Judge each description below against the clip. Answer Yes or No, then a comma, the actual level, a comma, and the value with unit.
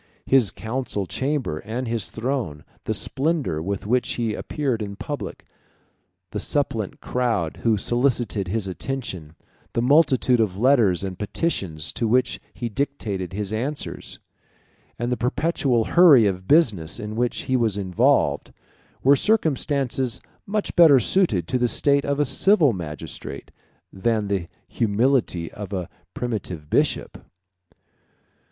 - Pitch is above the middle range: No, low, 115 Hz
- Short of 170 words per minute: Yes, slow, 135 wpm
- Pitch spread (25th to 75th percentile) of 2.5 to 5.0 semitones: No, wide, 5.4 semitones